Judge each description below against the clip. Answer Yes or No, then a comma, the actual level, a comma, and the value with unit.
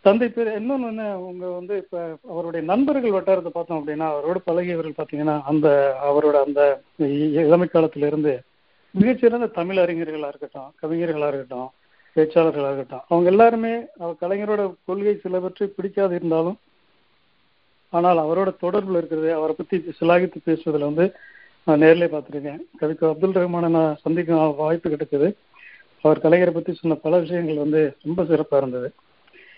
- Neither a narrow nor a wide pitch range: Yes, average, 3.1 semitones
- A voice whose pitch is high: No, medium, 165 Hz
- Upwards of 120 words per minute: Yes, fast, 130 wpm